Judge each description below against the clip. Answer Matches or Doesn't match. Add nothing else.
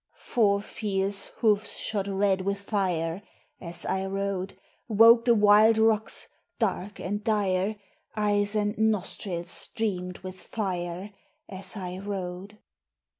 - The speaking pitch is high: Matches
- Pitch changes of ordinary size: Doesn't match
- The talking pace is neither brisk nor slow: Doesn't match